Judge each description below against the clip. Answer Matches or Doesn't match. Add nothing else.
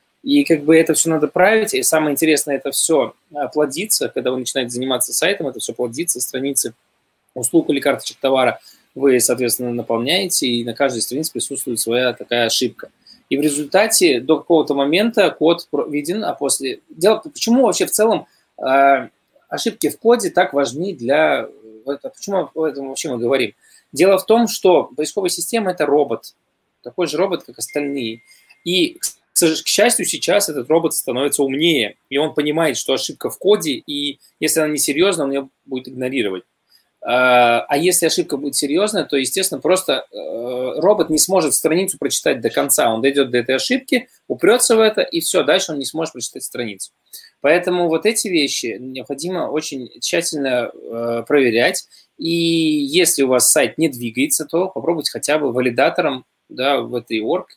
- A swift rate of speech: Matches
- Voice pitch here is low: Doesn't match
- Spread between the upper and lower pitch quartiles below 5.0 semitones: Doesn't match